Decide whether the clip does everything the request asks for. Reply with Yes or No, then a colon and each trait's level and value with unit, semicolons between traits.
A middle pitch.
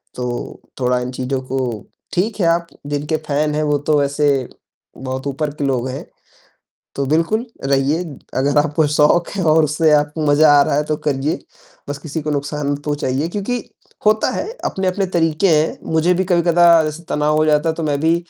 Yes: medium, 150 Hz